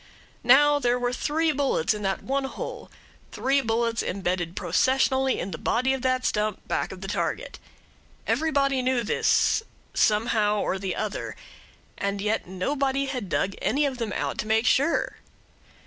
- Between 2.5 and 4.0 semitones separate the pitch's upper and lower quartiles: No, average, 4.5 semitones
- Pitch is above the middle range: Yes, high, 245 Hz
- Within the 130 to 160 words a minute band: Yes, average, 155 wpm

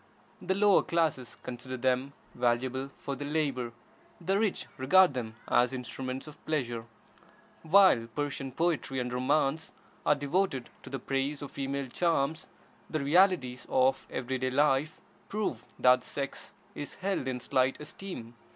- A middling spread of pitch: Yes, average, 3.6 semitones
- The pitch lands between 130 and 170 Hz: Yes, low, 135 Hz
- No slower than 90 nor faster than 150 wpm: Yes, average, 145 wpm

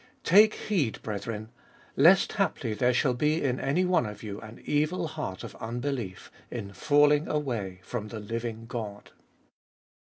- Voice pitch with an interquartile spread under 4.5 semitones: No, wide, 5.6 semitones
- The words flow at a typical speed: Yes, average, 150 wpm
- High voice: No, low, 120 Hz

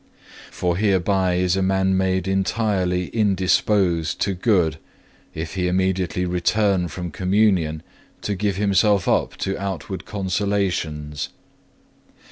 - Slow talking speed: Yes, slow, 110 wpm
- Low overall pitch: Yes, very low, 95 Hz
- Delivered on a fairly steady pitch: Yes, narrow, 1.9 semitones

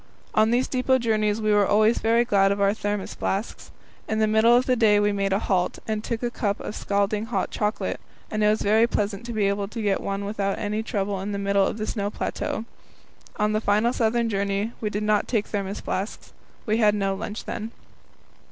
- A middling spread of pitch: No, narrow, 1.7 semitones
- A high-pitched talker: Yes, high, 210 Hz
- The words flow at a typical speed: No, fast, 220 wpm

